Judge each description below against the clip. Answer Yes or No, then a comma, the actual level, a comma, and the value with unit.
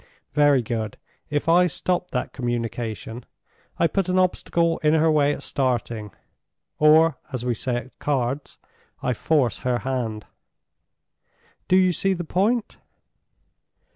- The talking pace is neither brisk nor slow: No, slow, 130 wpm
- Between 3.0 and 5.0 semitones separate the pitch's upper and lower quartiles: No, wide, 5.6 semitones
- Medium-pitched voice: Yes, medium, 145 Hz